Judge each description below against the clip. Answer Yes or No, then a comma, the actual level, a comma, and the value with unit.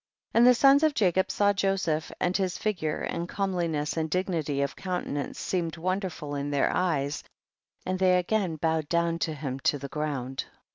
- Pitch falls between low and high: Yes, medium, 170 Hz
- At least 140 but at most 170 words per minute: No, average, 180 wpm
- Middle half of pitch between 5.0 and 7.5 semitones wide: No, average, 3.9 semitones